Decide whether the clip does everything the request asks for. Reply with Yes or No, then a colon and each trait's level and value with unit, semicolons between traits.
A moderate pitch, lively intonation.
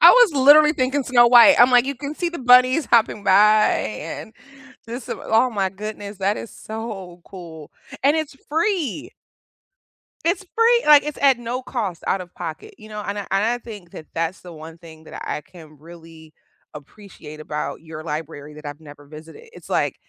No: high, 210 Hz; wide, 7.9 semitones